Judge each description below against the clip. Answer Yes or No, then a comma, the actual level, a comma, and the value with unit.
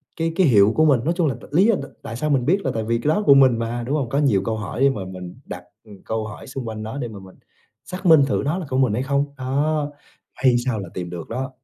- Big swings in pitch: No, average, 4.8 semitones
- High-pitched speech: No, low, 130 Hz